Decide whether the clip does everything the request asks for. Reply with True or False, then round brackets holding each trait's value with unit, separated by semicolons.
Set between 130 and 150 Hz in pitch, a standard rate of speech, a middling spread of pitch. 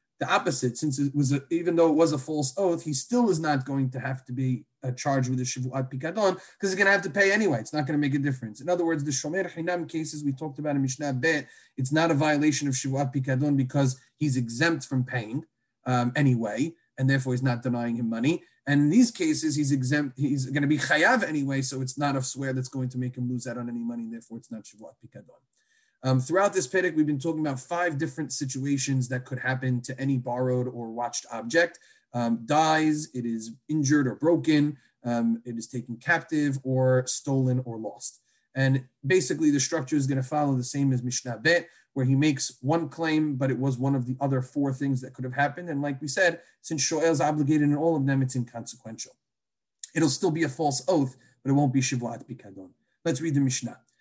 False (140 Hz; 230 wpm; 3.3 semitones)